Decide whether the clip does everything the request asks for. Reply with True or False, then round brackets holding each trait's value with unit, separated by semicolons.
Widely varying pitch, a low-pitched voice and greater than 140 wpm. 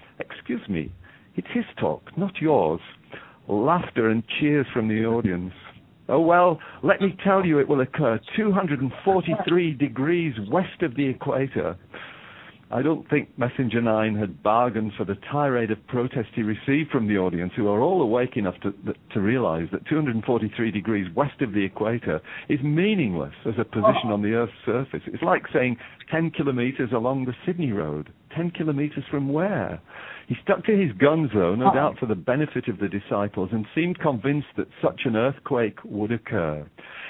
True (6.3 semitones; 130 Hz; 170 wpm)